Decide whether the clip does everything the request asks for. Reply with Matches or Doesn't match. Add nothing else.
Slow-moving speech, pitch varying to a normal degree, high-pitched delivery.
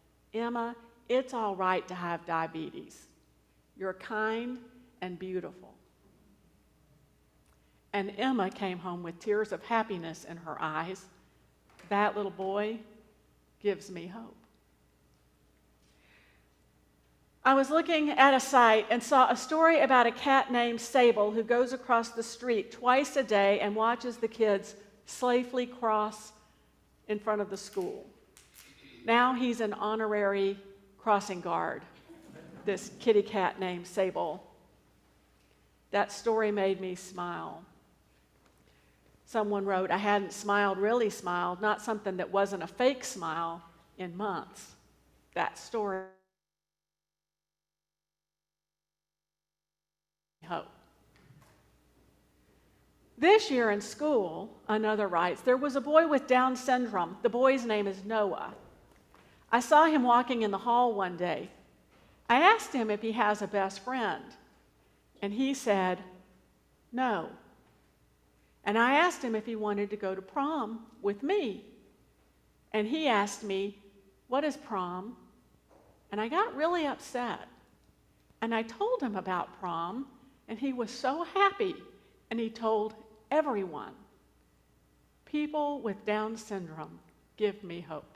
Matches